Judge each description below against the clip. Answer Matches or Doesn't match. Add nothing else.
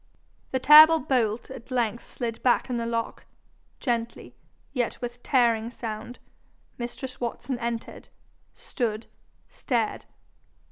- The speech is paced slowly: Matches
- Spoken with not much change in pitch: Matches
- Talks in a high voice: Matches